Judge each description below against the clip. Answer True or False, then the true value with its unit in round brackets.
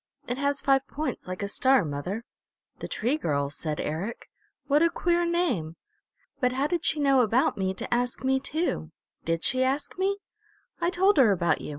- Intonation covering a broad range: True (8.0 semitones)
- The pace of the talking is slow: False (190 wpm)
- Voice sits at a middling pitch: False (260 Hz)